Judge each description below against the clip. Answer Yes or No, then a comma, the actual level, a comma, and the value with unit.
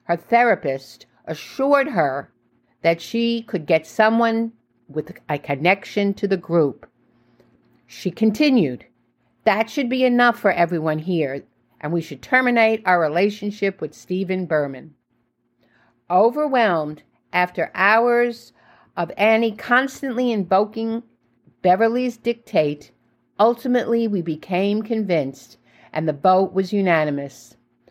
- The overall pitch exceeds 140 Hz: Yes, medium, 185 Hz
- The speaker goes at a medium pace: No, slow, 110 wpm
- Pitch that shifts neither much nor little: No, wide, 7.0 semitones